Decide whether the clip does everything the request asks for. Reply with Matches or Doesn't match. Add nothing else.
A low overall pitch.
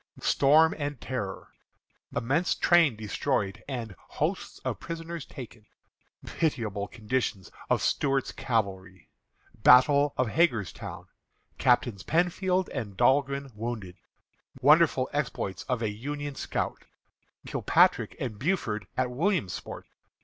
Matches